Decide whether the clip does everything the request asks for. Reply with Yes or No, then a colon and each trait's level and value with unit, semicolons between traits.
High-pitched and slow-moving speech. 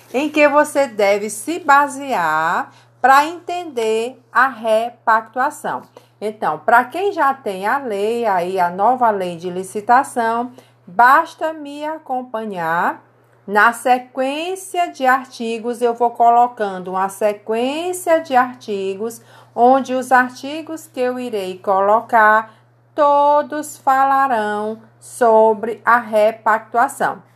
Yes: high, 235 Hz; slow, 105 wpm